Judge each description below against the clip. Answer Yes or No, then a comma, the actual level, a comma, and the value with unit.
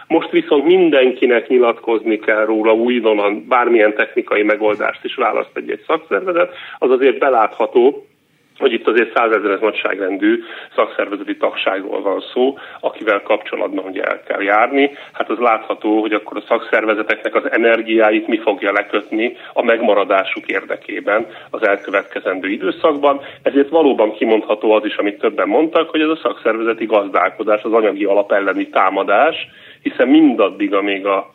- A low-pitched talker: No, medium, 155 Hz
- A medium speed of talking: Yes, average, 140 wpm